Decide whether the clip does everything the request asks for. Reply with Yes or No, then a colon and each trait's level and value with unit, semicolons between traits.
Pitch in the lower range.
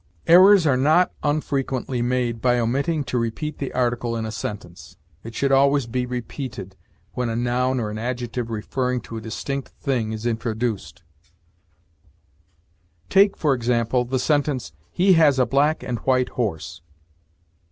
Yes: low, 125 Hz